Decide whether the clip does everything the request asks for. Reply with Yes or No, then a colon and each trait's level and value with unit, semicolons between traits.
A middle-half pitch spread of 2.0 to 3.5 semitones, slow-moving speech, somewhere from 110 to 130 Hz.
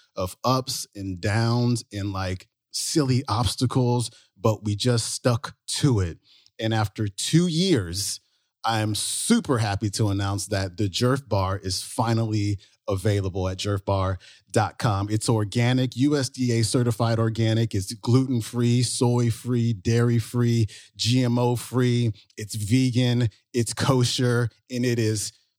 Yes: average, 2.9 semitones; slow, 125 wpm; low, 115 Hz